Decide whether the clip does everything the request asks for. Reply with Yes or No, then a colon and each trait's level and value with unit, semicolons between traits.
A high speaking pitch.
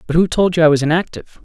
No: medium, 165 Hz